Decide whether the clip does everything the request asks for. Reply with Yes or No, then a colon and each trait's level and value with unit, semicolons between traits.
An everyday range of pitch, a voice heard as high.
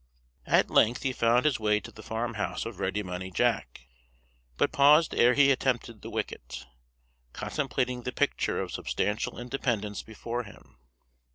No: average, 3.4 semitones; low, 115 Hz